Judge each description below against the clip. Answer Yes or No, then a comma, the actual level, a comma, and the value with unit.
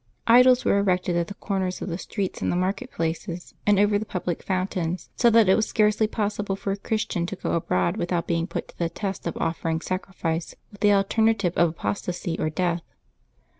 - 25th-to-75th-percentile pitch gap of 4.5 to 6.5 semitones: No, average, 3.2 semitones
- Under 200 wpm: No, fast, 205 wpm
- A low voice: No, medium, 185 Hz